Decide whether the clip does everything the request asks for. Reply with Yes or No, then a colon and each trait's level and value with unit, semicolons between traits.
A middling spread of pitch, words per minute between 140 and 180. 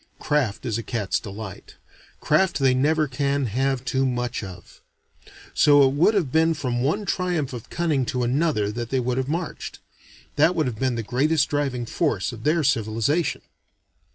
Yes: average, 4.0 semitones; average, 175 wpm